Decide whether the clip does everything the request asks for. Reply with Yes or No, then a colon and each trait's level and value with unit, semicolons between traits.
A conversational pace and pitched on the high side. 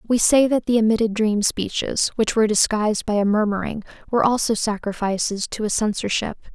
Yes: average, 175 wpm; high, 215 Hz